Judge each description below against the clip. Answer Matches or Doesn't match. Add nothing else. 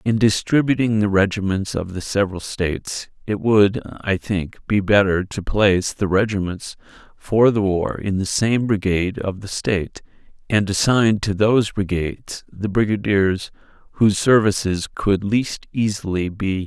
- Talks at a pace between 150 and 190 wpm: Matches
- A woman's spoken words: Doesn't match